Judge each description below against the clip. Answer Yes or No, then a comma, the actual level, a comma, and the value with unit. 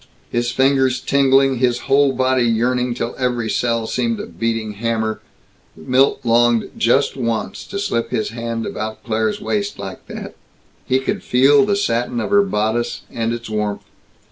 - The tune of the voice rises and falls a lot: No, average, 2.7 semitones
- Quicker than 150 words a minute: Yes, average, 160 wpm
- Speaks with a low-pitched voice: Yes, low, 120 Hz